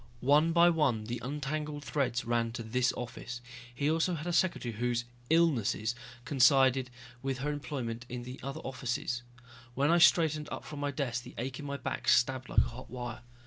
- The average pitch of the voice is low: Yes, low, 130 Hz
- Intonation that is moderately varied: Yes, average, 3.6 semitones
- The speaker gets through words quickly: No, average, 185 wpm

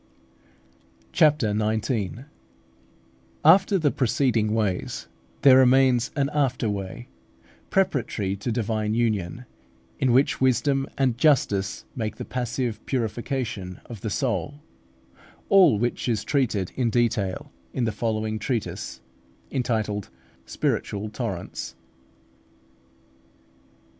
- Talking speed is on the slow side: Yes, slow, 110 wpm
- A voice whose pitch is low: Yes, low, 115 Hz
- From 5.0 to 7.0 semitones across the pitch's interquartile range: No, average, 3.7 semitones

